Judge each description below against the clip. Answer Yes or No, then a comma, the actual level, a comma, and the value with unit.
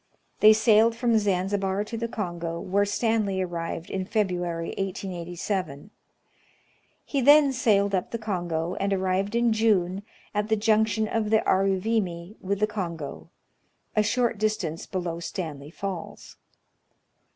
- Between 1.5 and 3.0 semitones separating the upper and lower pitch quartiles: No, average, 3.5 semitones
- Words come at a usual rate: No, slow, 130 wpm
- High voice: Yes, high, 200 Hz